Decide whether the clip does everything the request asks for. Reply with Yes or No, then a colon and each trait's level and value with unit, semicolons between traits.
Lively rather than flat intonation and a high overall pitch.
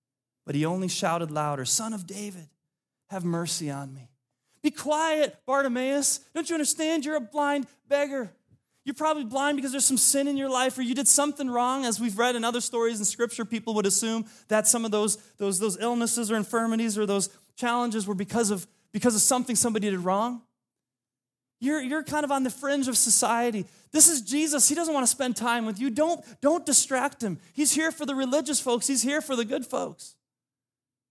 Yes: wide, 5.7 semitones; high, 235 Hz